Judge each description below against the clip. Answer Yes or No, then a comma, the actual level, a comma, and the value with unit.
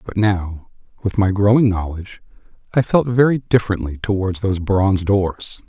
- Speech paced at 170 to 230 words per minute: No, average, 150 wpm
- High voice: No, low, 100 Hz